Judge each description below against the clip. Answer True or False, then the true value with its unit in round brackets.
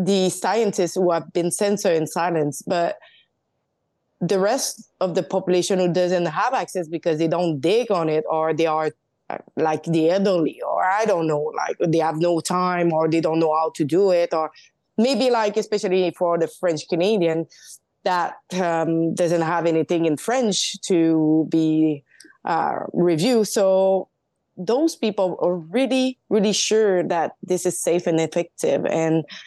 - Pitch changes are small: False (3.3 semitones)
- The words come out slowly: False (165 wpm)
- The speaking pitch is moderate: True (175 Hz)